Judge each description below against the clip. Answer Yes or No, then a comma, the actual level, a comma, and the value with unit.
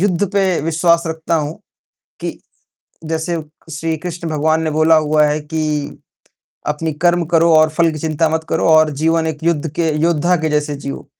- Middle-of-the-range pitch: Yes, medium, 160 Hz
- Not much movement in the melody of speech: Yes, narrow, 1.5 semitones